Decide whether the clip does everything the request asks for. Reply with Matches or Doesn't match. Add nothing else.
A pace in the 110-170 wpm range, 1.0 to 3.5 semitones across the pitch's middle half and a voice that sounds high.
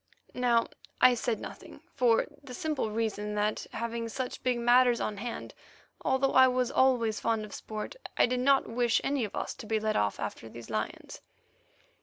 Doesn't match